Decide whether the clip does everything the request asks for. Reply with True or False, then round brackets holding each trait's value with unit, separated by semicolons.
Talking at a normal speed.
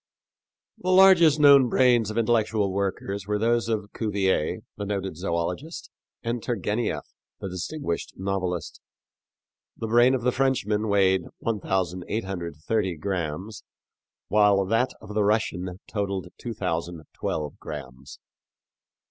False (110 wpm)